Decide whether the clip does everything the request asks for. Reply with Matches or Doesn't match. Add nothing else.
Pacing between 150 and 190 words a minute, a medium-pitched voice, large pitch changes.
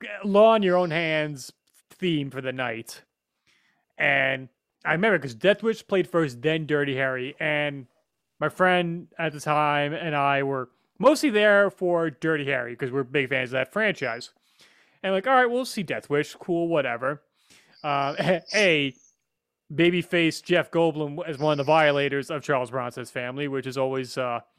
Doesn't match